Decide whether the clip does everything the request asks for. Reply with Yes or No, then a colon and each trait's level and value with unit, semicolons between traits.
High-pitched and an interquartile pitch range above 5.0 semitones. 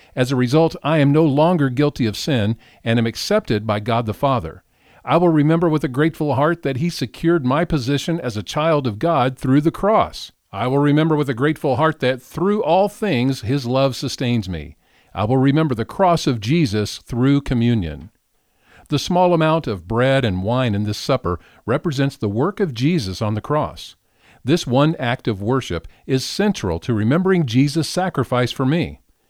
No: low, 135 Hz; wide, 5.4 semitones